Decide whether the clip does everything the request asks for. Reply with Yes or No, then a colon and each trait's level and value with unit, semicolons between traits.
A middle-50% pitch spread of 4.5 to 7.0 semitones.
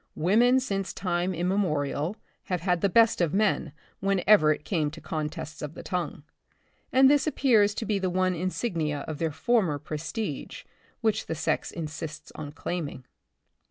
Yes: average, 4.8 semitones